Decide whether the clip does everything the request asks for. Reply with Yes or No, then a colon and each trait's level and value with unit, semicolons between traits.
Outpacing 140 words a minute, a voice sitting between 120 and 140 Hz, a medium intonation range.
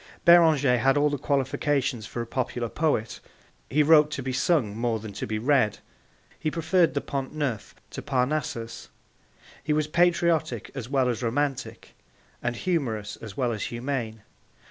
Yes: average, 160 wpm; low, 135 Hz; average, 4.4 semitones